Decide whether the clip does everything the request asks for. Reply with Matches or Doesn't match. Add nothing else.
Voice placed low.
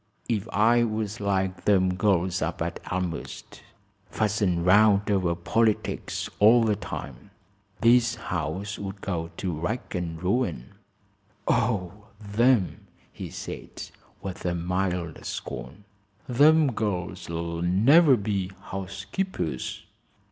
Matches